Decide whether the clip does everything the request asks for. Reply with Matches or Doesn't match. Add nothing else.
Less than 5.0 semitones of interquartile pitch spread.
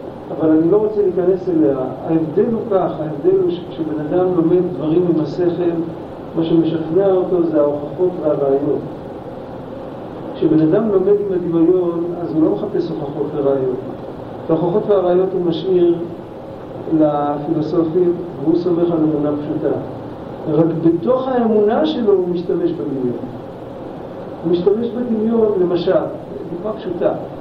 Matches